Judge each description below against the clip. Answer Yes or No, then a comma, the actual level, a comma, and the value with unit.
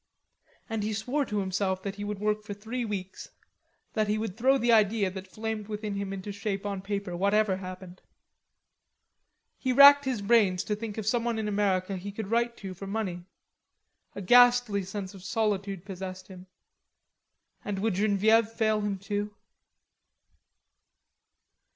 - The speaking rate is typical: Yes, average, 155 wpm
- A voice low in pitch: No, high, 205 Hz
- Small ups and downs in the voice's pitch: Yes, narrow, 2.3 semitones